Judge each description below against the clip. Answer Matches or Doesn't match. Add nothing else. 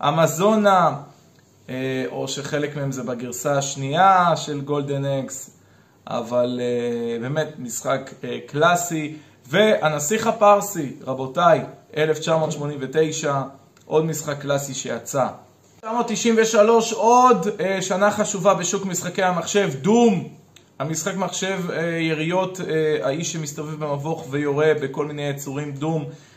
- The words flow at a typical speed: Doesn't match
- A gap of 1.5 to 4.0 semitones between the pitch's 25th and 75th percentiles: Doesn't match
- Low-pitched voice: Doesn't match